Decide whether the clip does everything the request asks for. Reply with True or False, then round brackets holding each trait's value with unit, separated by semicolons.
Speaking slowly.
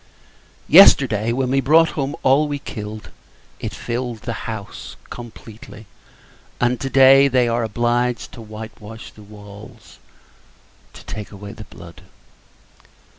True (130 wpm)